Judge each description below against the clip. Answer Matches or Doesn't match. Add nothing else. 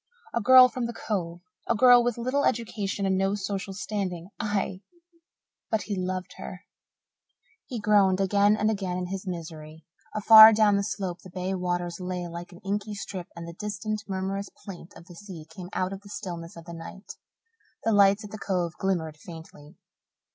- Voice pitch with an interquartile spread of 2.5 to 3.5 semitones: Matches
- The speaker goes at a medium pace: Matches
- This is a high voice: Matches